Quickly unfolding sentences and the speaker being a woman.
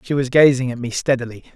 No: fast, 230 wpm; male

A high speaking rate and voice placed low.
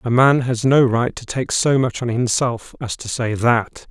Yes: fast, 230 wpm; low, 120 Hz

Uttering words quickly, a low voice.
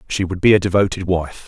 Yes: fast, 245 wpm; very low, 95 Hz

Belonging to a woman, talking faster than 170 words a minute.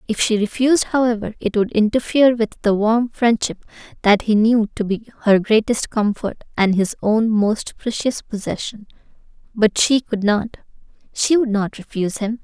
No: female; average, 165 wpm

